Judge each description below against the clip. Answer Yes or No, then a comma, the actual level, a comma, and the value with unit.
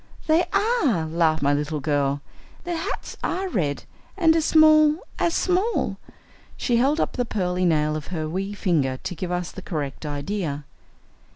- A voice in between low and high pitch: Yes, medium, 180 Hz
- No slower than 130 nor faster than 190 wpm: Yes, average, 165 wpm